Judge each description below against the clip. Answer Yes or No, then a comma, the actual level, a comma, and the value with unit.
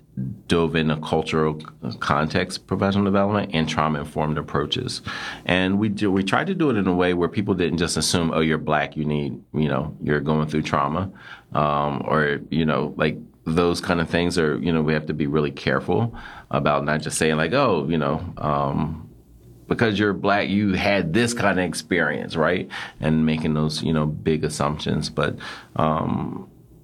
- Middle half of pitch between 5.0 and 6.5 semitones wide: No, average, 3.6 semitones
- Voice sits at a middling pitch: No, very low, 80 Hz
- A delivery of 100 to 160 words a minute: No, average, 190 wpm